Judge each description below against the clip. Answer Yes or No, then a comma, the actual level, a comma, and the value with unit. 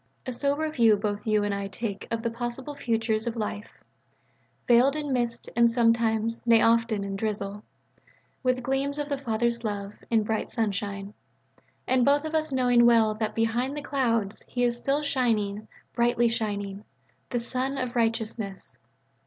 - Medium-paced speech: Yes, average, 160 wpm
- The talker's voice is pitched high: Yes, high, 230 Hz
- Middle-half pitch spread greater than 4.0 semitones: No, average, 2.8 semitones